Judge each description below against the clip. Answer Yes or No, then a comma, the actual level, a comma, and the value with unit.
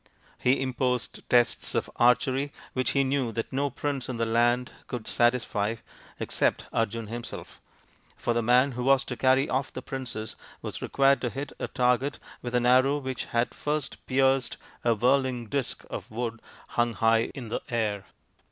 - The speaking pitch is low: Yes, low, 125 Hz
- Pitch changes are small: Yes, narrow, 2.3 semitones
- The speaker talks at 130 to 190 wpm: Yes, average, 170 wpm